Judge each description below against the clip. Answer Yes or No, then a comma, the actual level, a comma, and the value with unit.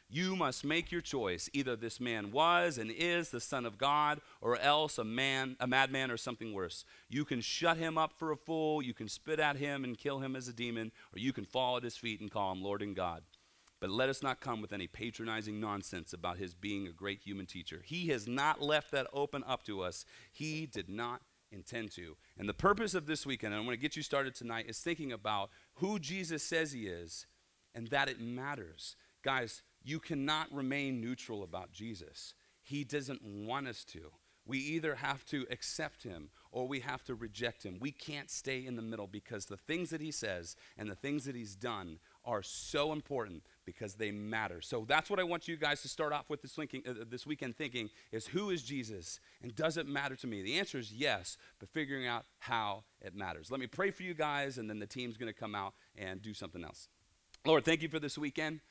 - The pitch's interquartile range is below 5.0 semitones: No, wide, 5.6 semitones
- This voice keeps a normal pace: No, fast, 225 wpm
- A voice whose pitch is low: Yes, low, 125 Hz